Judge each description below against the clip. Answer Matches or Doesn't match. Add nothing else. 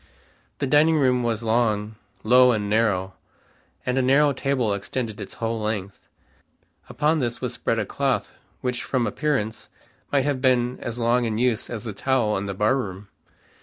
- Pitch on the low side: Matches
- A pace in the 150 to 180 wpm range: Matches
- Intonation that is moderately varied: Matches